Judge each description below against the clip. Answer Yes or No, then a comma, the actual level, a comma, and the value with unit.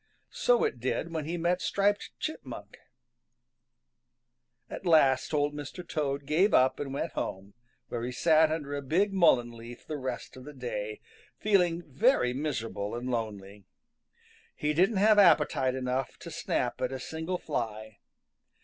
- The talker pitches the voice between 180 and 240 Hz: No, medium, 145 Hz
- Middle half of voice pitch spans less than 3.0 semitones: No, average, 5.3 semitones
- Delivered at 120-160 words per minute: Yes, average, 150 wpm